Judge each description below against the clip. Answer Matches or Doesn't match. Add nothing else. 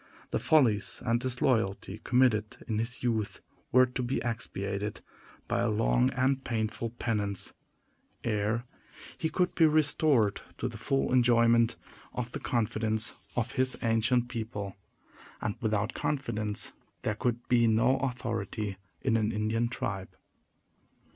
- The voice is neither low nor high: Doesn't match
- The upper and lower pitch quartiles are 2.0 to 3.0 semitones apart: Matches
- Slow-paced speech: Matches